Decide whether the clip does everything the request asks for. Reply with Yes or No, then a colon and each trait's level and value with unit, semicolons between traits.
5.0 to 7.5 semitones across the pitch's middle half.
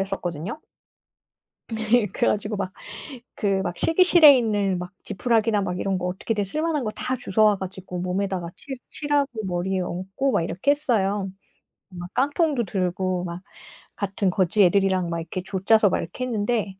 No: average, 3.8 semitones